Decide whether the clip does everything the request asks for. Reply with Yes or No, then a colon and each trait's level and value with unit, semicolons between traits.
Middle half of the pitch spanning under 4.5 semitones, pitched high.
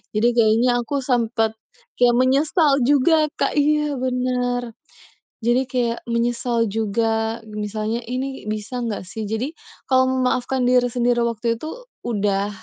Yes: narrow, 2.5 semitones; high, 240 Hz